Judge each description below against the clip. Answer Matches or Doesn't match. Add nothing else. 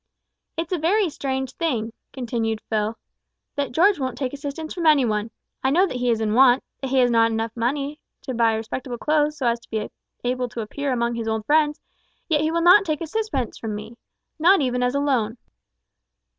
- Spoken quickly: Matches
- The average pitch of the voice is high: Matches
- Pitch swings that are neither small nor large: Matches